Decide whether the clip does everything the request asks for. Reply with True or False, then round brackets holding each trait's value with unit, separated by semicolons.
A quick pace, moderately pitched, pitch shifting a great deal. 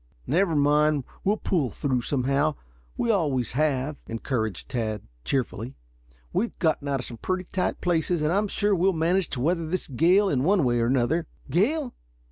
False (175 wpm; 155 Hz; 5.9 semitones)